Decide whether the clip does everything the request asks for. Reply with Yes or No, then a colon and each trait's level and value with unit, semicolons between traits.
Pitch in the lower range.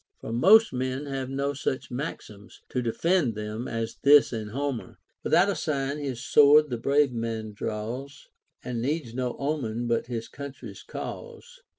Yes: low, 130 Hz